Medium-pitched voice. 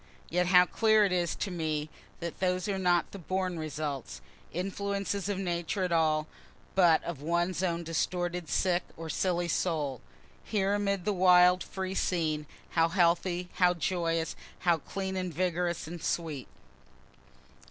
Yes: medium, 175 Hz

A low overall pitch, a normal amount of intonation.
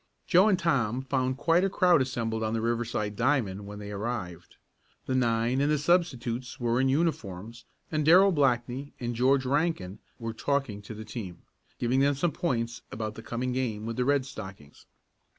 Yes: low, 125 Hz; average, 4.1 semitones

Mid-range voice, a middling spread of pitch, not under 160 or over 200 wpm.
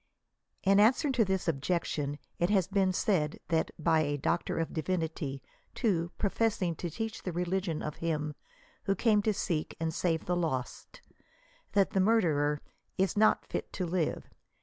Yes: medium, 175 Hz; average, 3.8 semitones; average, 165 wpm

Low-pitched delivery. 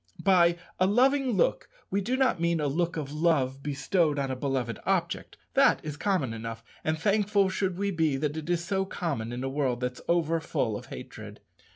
No: medium, 160 Hz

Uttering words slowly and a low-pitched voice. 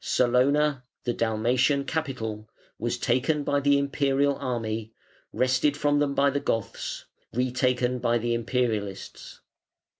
Yes: slow, 120 wpm; low, 125 Hz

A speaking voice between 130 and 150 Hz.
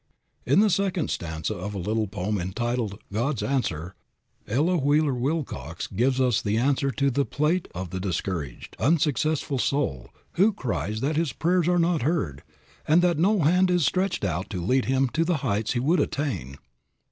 Yes: low, 135 Hz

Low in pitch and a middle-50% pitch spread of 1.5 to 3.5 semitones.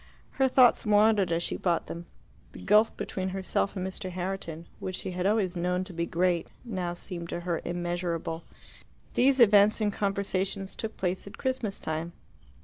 No: medium, 185 Hz; average, 2.9 semitones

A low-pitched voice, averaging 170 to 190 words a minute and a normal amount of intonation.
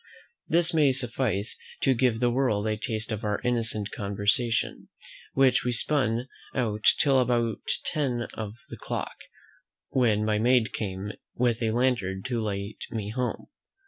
No: low, 115 Hz; average, 145 wpm; average, 3.0 semitones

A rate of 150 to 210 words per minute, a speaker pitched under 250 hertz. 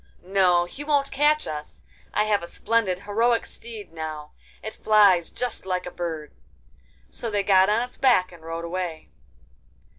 Yes: average, 160 wpm; high, 190 Hz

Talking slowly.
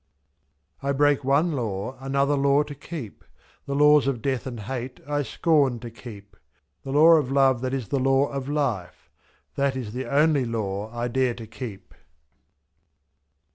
No: average, 170 wpm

